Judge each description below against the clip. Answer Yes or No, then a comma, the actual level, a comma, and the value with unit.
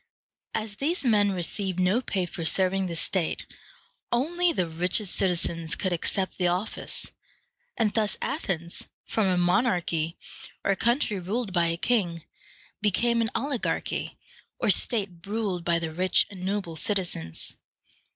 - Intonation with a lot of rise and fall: No, average, 4.0 semitones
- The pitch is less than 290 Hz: Yes, high, 190 Hz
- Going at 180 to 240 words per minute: No, average, 140 wpm